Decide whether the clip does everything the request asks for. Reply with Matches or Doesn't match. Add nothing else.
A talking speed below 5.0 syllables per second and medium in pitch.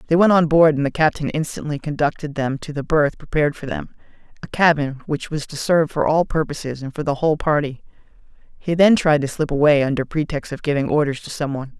Doesn't match